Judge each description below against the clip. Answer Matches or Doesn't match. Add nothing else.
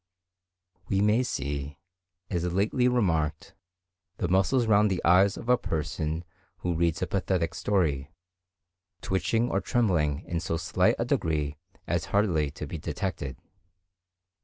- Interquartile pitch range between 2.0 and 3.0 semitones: Doesn't match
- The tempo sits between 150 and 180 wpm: Doesn't match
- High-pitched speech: Doesn't match